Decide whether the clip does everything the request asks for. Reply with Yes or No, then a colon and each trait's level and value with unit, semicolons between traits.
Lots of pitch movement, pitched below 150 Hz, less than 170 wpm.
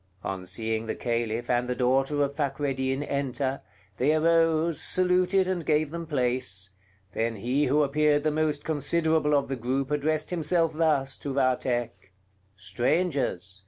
No: average, 4.2 semitones; medium, 140 Hz; average, 145 wpm